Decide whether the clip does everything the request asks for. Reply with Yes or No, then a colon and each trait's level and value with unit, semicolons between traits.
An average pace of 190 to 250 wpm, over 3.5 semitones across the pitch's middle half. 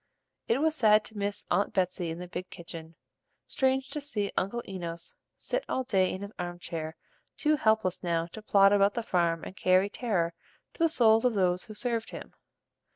Yes: average, 195 wpm; average, 4.5 semitones